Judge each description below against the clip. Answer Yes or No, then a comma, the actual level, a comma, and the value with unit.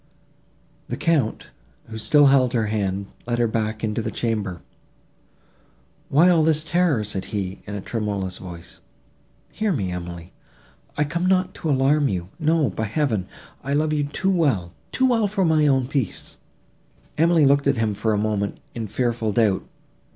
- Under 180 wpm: Yes, average, 165 wpm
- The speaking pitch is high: No, low, 120 Hz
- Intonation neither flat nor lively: No, wide, 6.8 semitones